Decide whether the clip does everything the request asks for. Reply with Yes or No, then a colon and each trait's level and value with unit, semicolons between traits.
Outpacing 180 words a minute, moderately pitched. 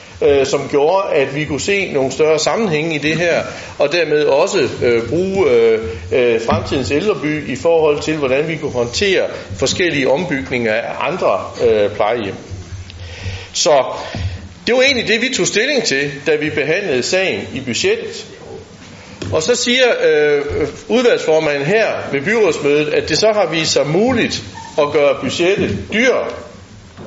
No: average, 150 wpm; medium, 175 Hz